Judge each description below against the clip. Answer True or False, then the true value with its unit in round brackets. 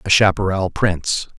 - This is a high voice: False (95 Hz)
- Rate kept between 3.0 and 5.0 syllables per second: True (4.9 syllables/s)